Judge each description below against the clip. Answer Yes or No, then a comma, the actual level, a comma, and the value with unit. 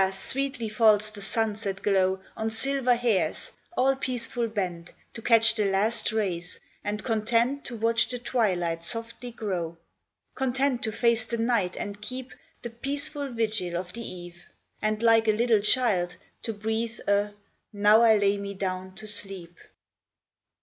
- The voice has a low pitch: No, high, 220 Hz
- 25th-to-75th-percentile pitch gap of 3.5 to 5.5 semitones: No, average, 3.0 semitones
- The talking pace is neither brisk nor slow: Yes, average, 155 wpm